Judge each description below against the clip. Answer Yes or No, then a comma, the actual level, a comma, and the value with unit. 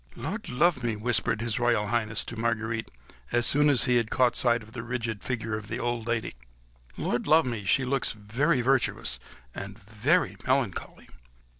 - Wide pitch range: No, narrow, 2.5 semitones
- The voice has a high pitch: No, low, 120 Hz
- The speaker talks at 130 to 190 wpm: Yes, average, 175 wpm